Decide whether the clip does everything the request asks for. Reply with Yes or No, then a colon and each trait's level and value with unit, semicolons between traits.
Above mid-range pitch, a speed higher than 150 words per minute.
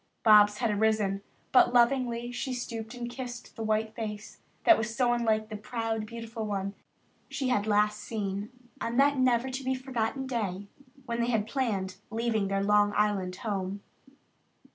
Yes: high, 225 Hz; average, 165 wpm